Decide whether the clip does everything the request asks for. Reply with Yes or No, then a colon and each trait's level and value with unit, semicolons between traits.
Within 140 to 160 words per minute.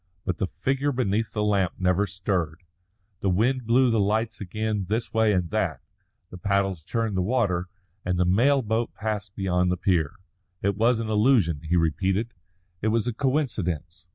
No: average, 170 wpm